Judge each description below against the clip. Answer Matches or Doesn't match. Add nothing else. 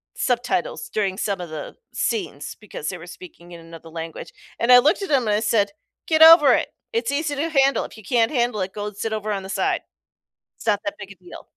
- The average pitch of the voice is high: Matches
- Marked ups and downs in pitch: Matches